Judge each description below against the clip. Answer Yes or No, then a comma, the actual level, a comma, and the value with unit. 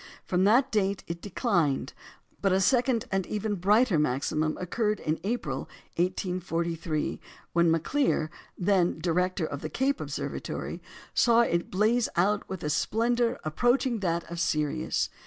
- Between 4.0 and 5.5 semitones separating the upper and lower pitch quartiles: Yes, average, 5.2 semitones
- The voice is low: No, medium, 185 Hz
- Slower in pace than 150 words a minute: Yes, average, 140 wpm